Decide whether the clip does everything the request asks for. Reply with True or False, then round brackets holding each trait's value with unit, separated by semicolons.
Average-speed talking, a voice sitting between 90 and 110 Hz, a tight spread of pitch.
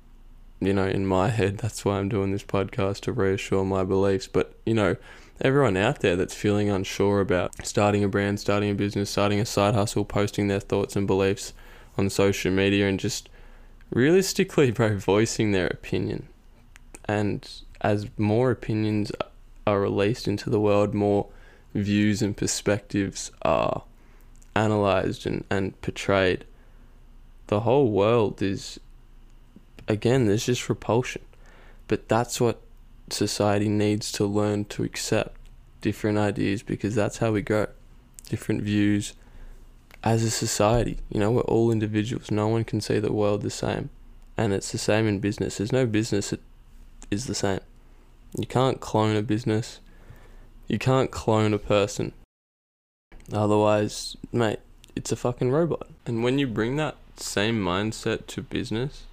True (150 wpm; 105 Hz; 2.1 semitones)